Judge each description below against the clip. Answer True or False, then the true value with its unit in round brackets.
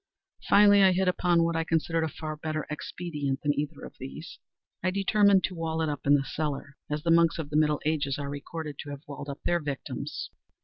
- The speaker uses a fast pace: True (215 wpm)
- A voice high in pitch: False (155 Hz)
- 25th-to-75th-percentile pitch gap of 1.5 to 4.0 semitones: True (2.7 semitones)